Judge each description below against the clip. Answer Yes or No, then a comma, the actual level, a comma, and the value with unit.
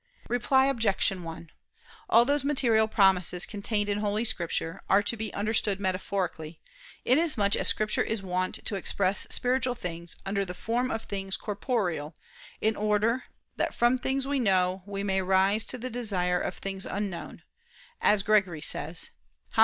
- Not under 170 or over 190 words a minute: No, average, 155 wpm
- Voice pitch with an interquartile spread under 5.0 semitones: Yes, average, 3.5 semitones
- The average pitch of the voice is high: Yes, high, 205 Hz